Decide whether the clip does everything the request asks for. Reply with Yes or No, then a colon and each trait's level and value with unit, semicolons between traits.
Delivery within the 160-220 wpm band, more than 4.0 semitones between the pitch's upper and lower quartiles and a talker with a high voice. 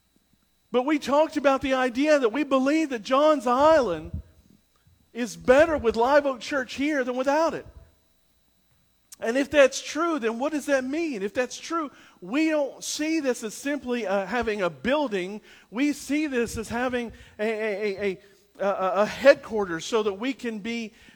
Yes: average, 170 wpm; average, 4.7 semitones; very high, 255 Hz